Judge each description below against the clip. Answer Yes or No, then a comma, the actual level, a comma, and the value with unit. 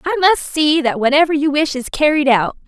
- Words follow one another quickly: Yes, fast, 225 wpm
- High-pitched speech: Yes, very high, 295 Hz